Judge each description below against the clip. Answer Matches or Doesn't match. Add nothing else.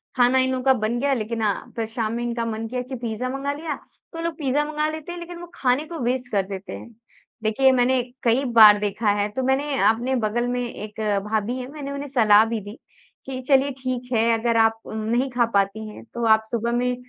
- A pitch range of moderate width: Matches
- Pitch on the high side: Matches